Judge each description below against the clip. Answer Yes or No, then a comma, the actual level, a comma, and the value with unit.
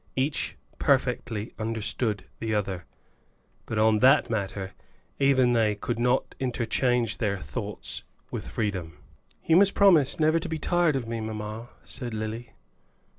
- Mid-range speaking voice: No, low, 115 Hz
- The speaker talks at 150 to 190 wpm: No, slow, 135 wpm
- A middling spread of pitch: Yes, average, 3.8 semitones